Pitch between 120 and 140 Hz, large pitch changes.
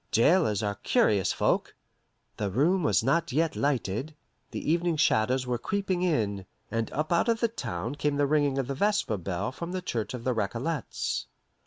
Yes: low, 135 Hz; wide, 7.3 semitones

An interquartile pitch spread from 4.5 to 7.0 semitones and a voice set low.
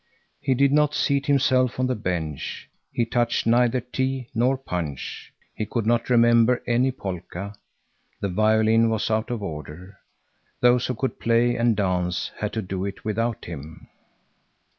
No: average, 4.1 semitones; low, 115 Hz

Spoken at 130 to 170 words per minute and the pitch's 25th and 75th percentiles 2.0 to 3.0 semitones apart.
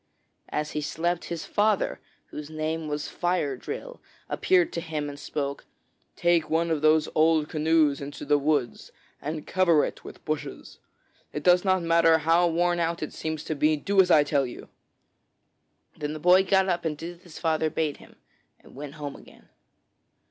No: average, 180 wpm; narrow, 2.4 semitones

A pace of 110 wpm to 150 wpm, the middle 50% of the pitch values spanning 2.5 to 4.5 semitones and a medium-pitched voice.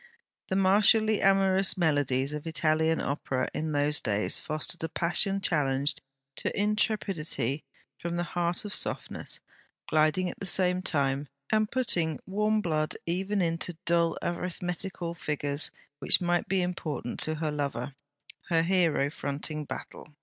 Yes: slow, 135 wpm; average, 4.0 semitones; medium, 170 Hz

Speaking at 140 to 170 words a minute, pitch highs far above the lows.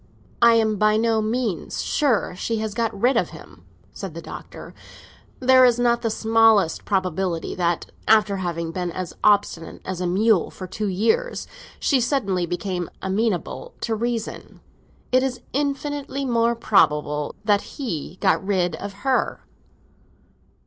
No: average, 145 wpm; average, 4.3 semitones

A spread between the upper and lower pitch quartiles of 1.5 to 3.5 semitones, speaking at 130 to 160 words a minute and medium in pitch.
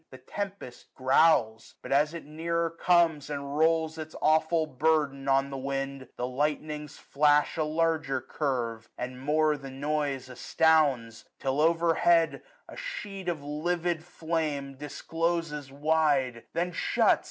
Yes: average, 3.1 semitones; average, 140 wpm; medium, 150 Hz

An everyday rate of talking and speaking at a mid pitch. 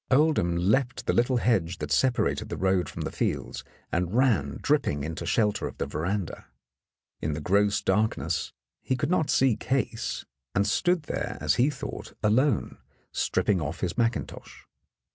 No: average, 160 wpm; low, 105 Hz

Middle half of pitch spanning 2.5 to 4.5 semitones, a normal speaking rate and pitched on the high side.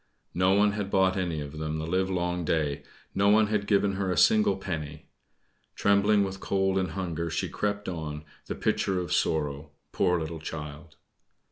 No: average, 3.9 semitones; average, 170 wpm; very low, 90 Hz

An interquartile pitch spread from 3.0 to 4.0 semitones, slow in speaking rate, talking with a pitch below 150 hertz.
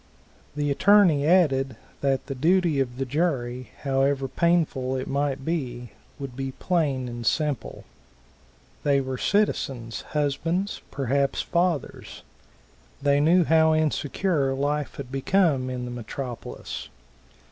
Yes: average, 3.5 semitones; slow, 120 wpm; medium, 140 Hz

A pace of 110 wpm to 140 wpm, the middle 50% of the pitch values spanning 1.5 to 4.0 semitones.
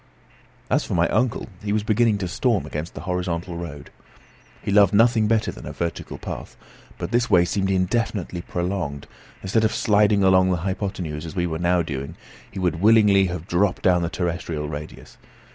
No: average, 185 wpm; average, 3.3 semitones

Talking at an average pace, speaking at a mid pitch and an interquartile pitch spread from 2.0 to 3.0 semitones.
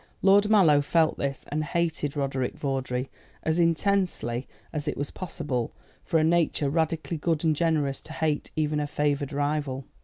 Yes: average, 160 wpm; medium, 150 Hz; average, 2.7 semitones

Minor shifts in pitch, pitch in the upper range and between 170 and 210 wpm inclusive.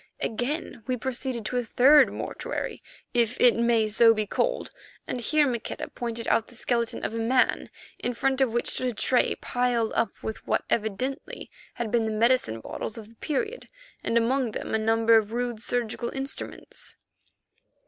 Yes: narrow, 2.1 semitones; high, 235 Hz; average, 175 wpm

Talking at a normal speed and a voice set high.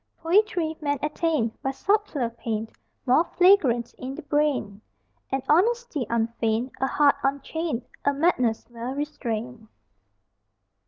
No: slow, 115 wpm; very high, 275 Hz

